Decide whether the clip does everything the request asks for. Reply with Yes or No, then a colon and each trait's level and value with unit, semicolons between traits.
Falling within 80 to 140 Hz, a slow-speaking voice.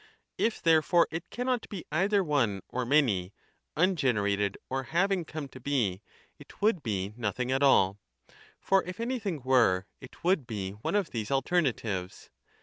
No: low, 135 Hz; average, 155 wpm